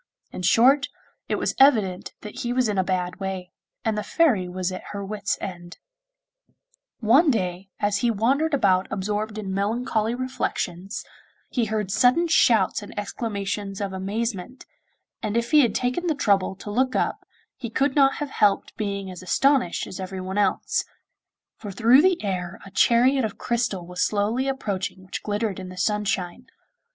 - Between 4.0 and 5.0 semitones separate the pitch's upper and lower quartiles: Yes, average, 4.4 semitones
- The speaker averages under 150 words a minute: No, average, 165 wpm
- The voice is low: No, high, 210 Hz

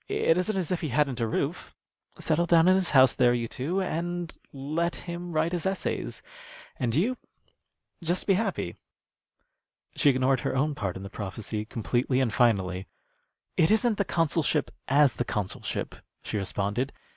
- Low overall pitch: No, medium, 145 Hz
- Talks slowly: No, average, 165 wpm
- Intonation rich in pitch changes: Yes, wide, 6.6 semitones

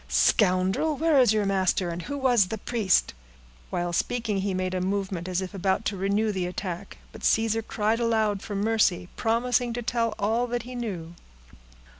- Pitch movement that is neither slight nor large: Yes, average, 3.7 semitones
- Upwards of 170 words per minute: Yes, average, 180 wpm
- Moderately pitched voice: No, high, 205 Hz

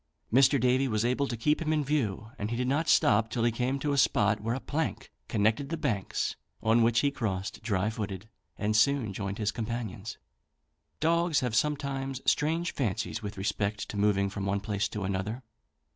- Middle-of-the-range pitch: No, low, 115 Hz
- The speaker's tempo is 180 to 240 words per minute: Yes, average, 190 wpm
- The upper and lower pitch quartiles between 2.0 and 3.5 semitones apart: No, average, 4.9 semitones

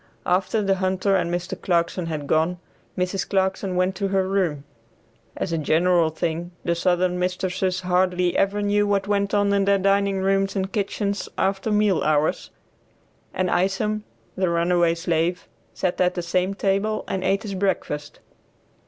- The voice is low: No, medium, 185 Hz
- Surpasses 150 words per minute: Yes, average, 160 wpm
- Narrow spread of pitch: Yes, narrow, 2.0 semitones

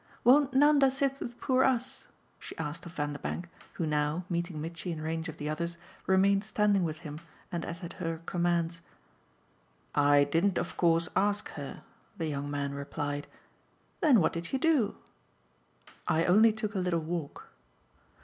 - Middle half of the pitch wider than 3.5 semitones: Yes, average, 5.0 semitones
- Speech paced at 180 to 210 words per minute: No, average, 160 wpm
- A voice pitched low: No, medium, 170 Hz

